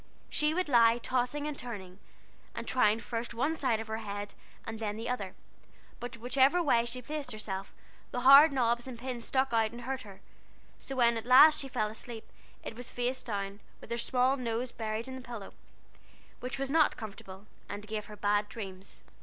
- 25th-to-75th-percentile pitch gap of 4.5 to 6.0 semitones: No, average, 3.2 semitones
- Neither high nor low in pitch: No, high, 235 Hz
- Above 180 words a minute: Yes, average, 195 wpm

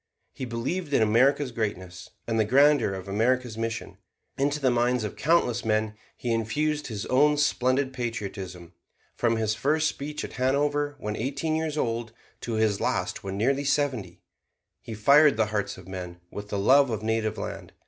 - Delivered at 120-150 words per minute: No, average, 170 wpm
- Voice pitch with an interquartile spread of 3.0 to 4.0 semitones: No, average, 4.7 semitones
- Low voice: Yes, low, 120 Hz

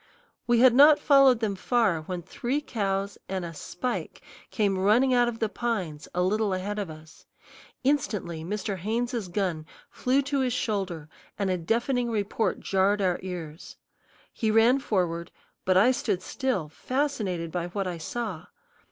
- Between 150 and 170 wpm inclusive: Yes, average, 160 wpm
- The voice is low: No, high, 205 Hz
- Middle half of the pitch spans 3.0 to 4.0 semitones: No, average, 5.0 semitones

